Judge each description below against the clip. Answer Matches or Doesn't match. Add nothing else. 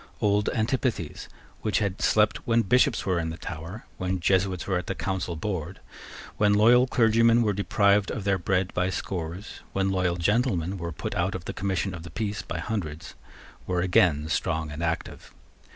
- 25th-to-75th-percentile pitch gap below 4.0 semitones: Matches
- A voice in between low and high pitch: Doesn't match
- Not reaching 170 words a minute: Doesn't match